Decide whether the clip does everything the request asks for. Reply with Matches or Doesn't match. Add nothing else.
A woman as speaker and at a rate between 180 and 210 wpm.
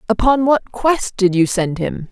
Matches